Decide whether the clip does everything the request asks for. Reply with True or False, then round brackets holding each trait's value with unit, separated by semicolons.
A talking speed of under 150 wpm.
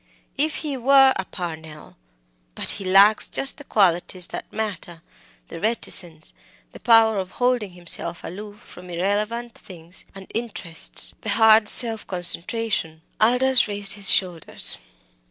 True (135 wpm)